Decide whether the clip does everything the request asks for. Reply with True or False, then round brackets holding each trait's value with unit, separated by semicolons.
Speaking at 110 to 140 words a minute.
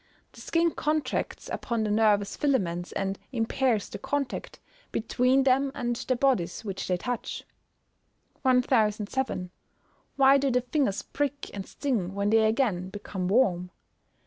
True (135 wpm)